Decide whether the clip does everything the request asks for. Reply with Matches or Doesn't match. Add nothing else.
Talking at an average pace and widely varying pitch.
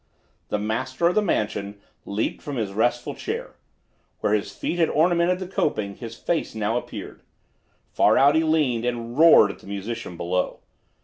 Matches